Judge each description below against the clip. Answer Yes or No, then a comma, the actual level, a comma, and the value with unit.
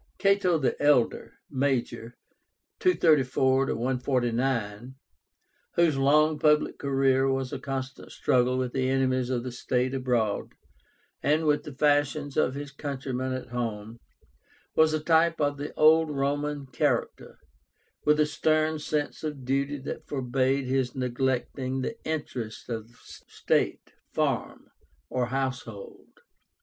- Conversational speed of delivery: No, slow, 125 wpm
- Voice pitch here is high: No, low, 135 Hz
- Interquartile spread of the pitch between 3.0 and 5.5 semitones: No, narrow, 2.6 semitones